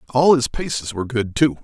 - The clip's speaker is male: Yes, male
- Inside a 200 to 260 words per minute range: Yes, fast, 220 wpm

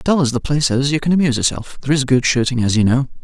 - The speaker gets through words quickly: Yes, fast, 295 wpm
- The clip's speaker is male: Yes, male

